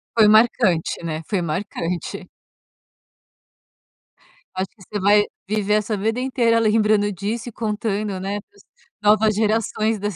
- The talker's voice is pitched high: Yes, high, 210 Hz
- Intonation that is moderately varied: No, narrow, 2.0 semitones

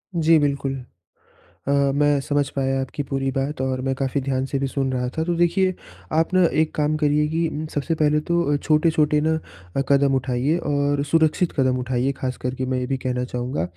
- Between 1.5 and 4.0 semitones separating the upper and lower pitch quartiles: Yes, average, 2.7 semitones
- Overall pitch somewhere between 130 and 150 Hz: Yes, medium, 140 Hz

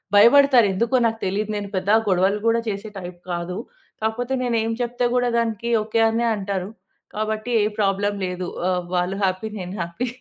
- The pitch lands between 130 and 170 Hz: No, high, 210 Hz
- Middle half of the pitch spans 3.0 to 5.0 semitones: Yes, average, 3.5 semitones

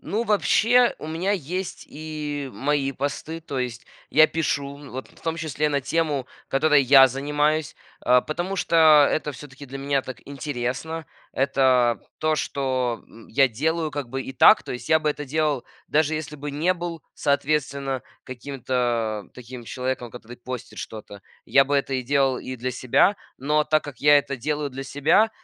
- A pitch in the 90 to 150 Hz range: Yes, medium, 140 Hz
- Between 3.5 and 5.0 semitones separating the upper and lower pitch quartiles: No, average, 3.1 semitones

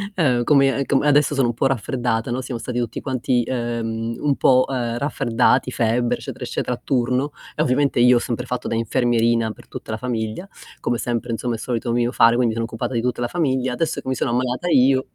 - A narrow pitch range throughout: Yes, narrow, 2.0 semitones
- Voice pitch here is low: Yes, low, 125 Hz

